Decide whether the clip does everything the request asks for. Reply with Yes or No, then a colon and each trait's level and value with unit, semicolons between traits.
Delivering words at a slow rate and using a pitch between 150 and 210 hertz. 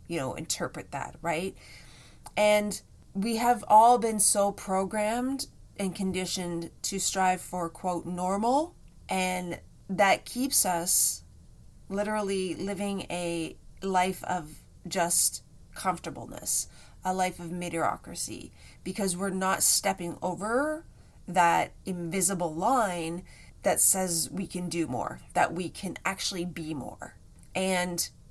Yes: slow, 115 wpm; medium, 185 Hz